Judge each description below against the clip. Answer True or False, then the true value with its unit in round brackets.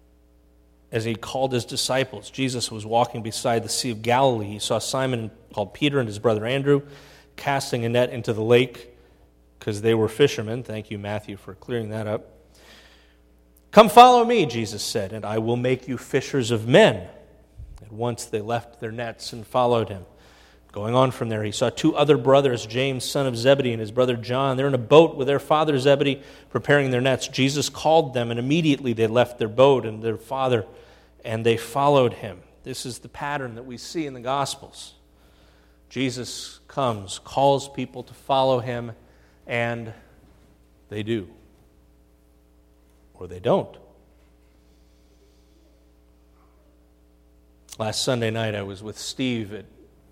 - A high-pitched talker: False (115 Hz)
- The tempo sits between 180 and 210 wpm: False (165 wpm)